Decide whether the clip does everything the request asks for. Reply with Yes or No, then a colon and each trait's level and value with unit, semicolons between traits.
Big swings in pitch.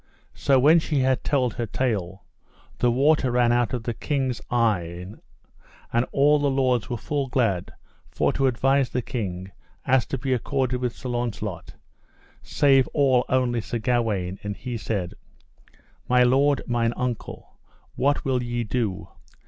No: average, 2.8 semitones